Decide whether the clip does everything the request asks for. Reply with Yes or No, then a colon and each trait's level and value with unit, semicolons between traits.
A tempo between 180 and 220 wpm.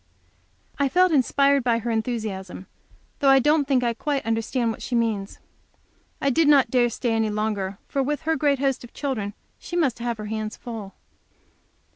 Yes: average, 185 wpm